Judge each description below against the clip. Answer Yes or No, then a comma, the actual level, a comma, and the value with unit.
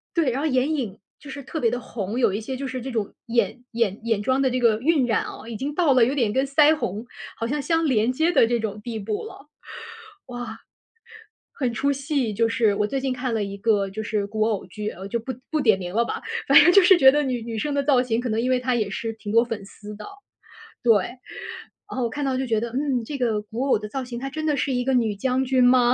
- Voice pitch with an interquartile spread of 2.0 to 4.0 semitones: Yes, average, 3.5 semitones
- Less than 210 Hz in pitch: No, high, 245 Hz